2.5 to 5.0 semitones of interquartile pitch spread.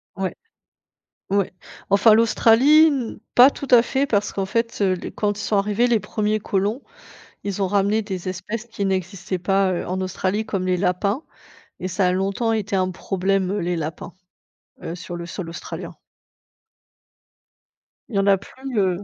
Yes: average, 2.9 semitones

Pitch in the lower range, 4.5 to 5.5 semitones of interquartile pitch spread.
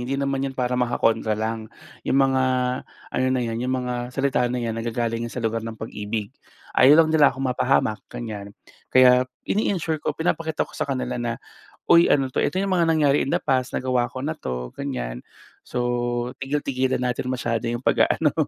No: low, 125 Hz; average, 2.8 semitones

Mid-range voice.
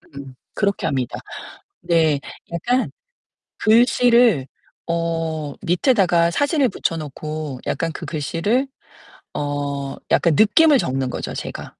Yes: medium, 165 Hz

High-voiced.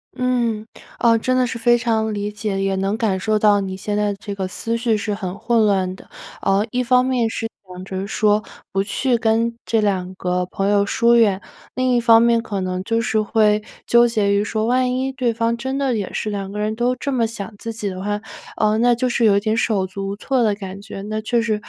Yes: high, 215 Hz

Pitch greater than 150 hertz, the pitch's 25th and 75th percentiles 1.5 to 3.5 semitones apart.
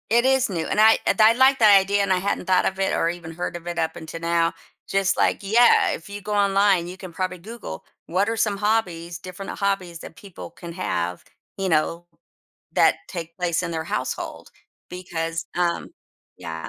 Yes: medium, 185 Hz; average, 3.1 semitones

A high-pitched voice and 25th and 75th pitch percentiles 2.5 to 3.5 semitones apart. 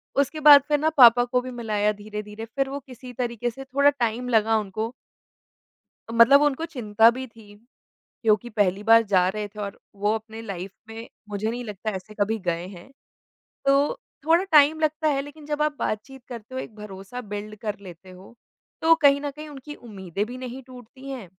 No: high, 230 Hz; average, 4.6 semitones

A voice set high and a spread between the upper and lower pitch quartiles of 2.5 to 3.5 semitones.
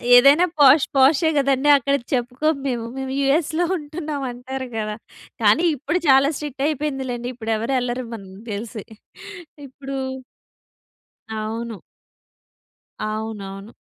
No: very high, 265 Hz; average, 3.9 semitones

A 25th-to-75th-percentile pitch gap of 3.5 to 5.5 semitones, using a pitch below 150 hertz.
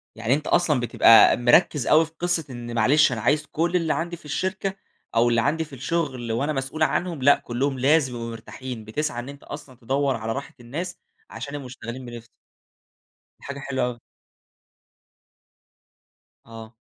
Yes: average, 4.3 semitones; low, 135 Hz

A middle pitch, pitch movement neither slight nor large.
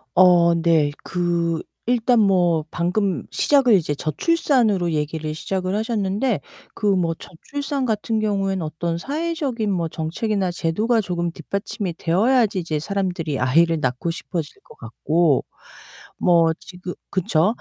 Yes: medium, 180 Hz; average, 4.5 semitones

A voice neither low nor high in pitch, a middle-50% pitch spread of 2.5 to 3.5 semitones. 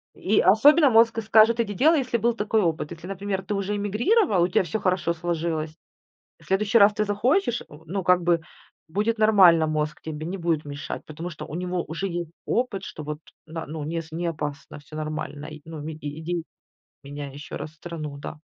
No: medium, 175 Hz; average, 5.0 semitones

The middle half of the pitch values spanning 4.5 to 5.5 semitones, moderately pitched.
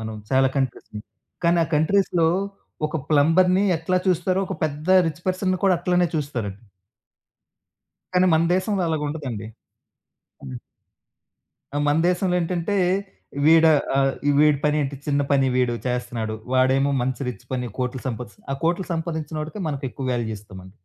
Yes: average, 5.2 semitones; medium, 150 Hz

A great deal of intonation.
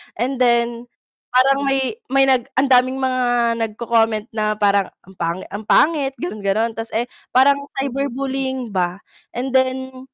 No: average, 3.2 semitones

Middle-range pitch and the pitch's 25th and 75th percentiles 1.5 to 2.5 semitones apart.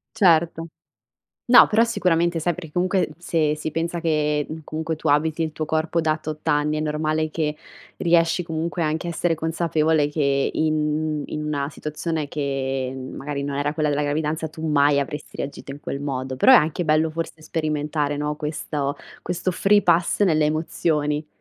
Yes: medium, 155 Hz; narrow, 1.8 semitones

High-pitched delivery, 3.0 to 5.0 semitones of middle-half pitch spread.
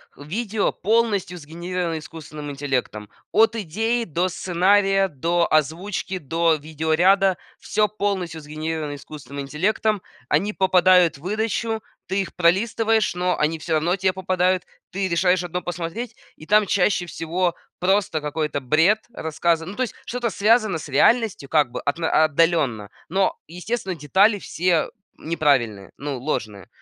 No: medium, 175 Hz; average, 4.2 semitones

